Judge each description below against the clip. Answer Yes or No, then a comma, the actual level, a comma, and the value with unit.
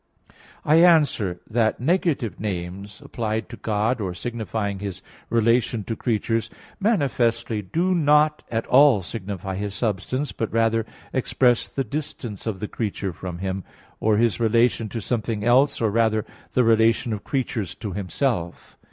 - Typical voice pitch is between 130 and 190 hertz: No, low, 115 Hz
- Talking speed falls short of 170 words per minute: Yes, average, 145 wpm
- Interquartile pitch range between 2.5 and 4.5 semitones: Yes, average, 3.3 semitones